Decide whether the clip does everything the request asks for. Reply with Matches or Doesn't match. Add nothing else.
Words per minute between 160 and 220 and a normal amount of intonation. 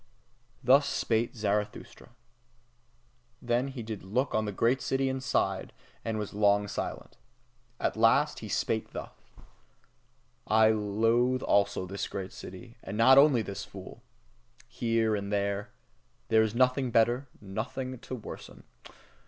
Doesn't match